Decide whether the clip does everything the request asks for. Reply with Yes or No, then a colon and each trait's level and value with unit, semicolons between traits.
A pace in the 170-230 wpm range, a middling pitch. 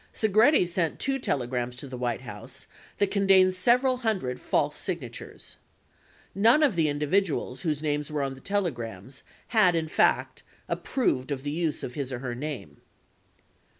No: average, 155 wpm; medium, 155 Hz